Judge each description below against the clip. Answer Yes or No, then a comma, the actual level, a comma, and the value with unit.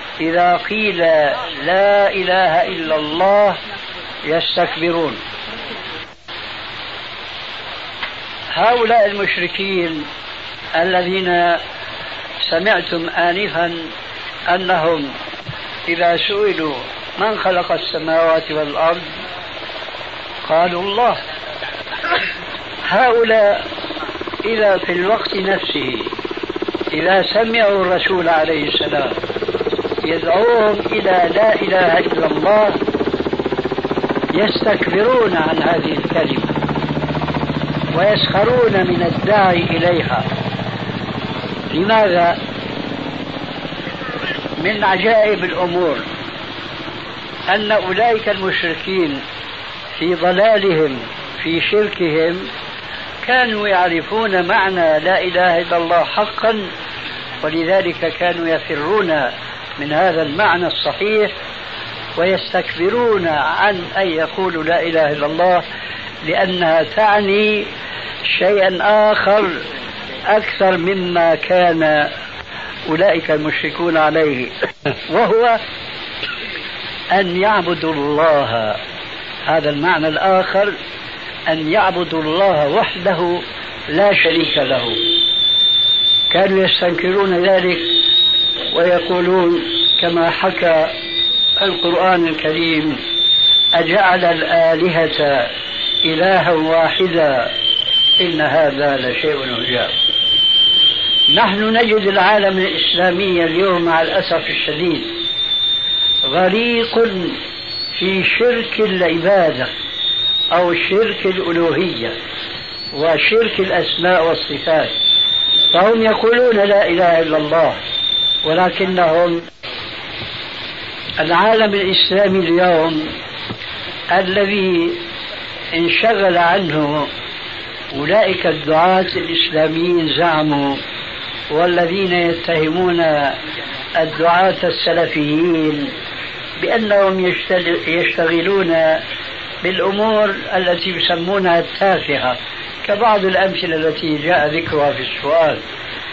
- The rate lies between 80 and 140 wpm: No, average, 70 wpm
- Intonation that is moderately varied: Yes, average, 3.7 semitones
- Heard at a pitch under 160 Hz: No, medium, 180 Hz